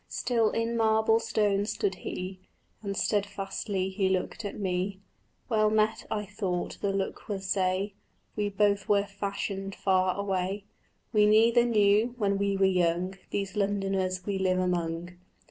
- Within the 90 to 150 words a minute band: Yes, average, 145 wpm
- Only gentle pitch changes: Yes, narrow, 1.9 semitones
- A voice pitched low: No, high, 200 Hz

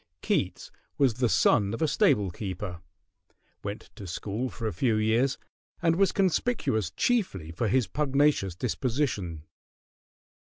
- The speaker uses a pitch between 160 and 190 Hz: No, low, 115 Hz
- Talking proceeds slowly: Yes, slow, 130 wpm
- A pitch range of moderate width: No, wide, 6.3 semitones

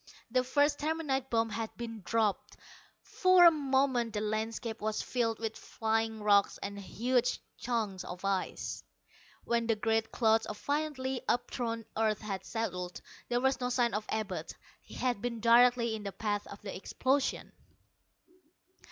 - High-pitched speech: Yes, high, 230 Hz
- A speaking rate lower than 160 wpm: Yes, average, 150 wpm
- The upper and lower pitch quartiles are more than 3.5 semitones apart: No, average, 2.8 semitones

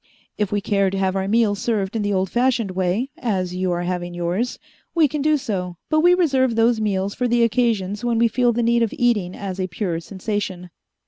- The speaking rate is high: Yes, fast, 220 wpm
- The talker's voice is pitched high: Yes, high, 205 Hz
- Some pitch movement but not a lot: Yes, average, 4.2 semitones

